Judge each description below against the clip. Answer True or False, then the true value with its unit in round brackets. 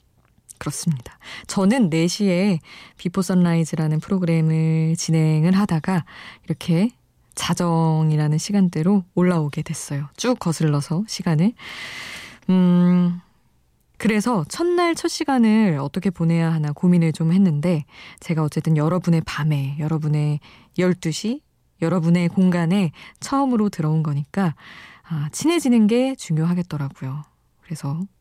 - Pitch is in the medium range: True (170 Hz)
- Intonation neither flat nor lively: True (3.5 semitones)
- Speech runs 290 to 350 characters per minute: False (275 characters per minute)